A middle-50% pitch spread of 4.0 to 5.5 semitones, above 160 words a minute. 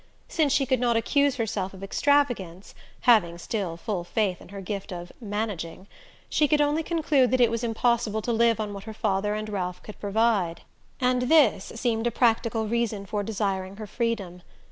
No: average, 3.5 semitones; average, 185 wpm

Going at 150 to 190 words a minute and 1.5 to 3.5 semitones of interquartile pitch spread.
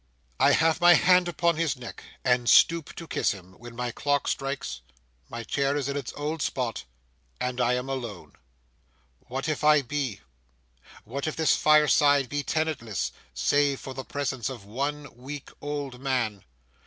Yes: average, 165 wpm; average, 3.2 semitones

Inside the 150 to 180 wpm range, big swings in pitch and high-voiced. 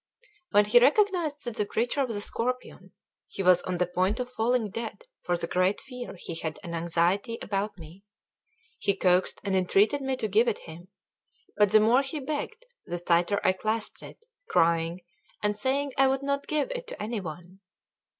No: average, 190 wpm; wide, 6.1 semitones; high, 210 Hz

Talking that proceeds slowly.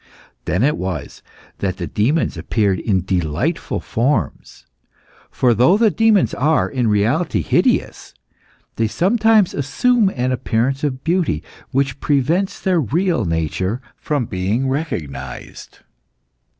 Yes: slow, 120 wpm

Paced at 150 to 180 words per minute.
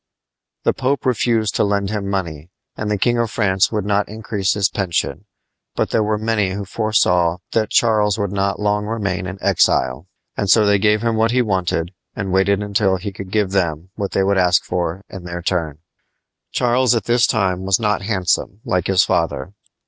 No: average, 195 wpm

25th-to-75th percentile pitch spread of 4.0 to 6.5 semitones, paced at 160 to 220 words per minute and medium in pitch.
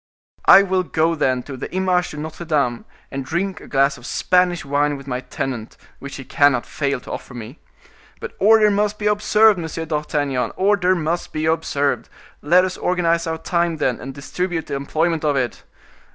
Yes: average, 4.6 semitones; average, 185 wpm; medium, 160 Hz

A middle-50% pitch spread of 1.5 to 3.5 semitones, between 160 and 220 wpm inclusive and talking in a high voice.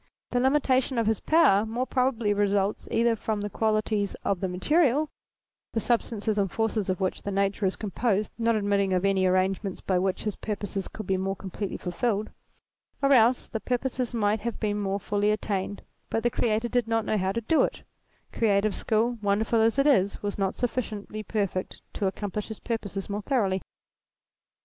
Yes: average, 2.8 semitones; average, 185 wpm; high, 210 Hz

